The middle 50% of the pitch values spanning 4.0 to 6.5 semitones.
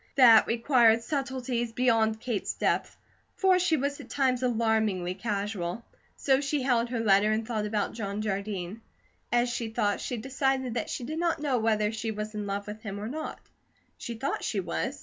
No: average, 3.3 semitones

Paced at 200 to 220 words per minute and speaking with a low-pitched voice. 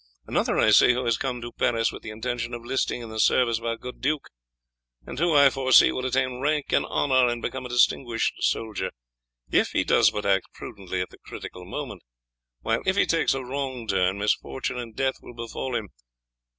Yes: fast, 205 wpm; low, 120 Hz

